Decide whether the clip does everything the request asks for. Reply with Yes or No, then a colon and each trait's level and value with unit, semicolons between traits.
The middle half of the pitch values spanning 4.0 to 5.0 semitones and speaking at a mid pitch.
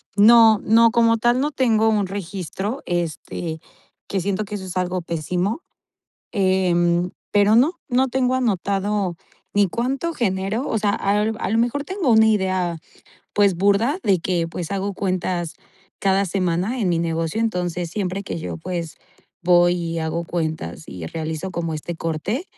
No: average, 4.3 semitones; high, 195 Hz